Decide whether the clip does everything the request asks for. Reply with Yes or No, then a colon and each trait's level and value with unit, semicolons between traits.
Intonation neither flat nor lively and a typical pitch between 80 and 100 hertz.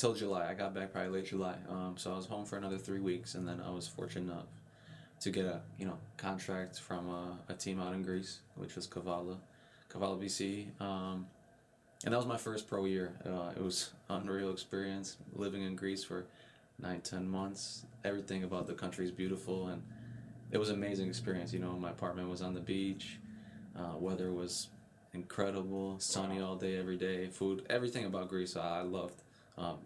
No: narrow, 1.4 semitones; very low, 95 Hz